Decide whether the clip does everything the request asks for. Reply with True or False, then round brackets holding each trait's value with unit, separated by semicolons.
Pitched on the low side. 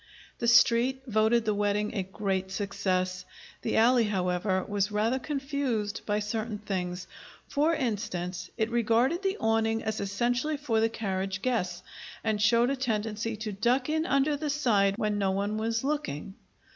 False (220 Hz)